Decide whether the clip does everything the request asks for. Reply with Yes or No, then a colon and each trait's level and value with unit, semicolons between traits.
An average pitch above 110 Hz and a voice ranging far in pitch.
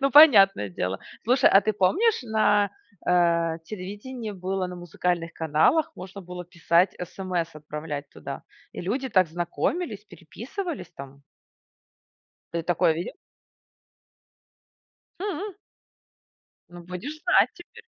Yes: medium, 185 Hz; wide, 6.6 semitones